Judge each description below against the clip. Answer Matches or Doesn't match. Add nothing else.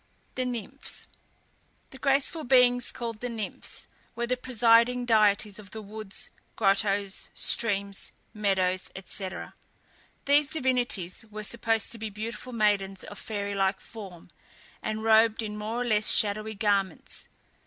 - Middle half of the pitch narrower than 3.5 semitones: Matches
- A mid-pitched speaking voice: Doesn't match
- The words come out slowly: Matches